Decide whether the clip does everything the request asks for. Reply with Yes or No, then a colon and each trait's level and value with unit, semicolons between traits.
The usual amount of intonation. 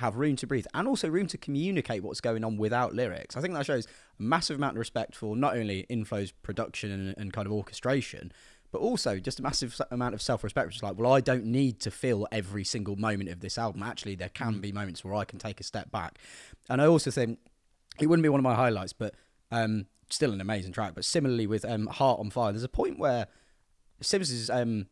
Yes: average, 4.0 semitones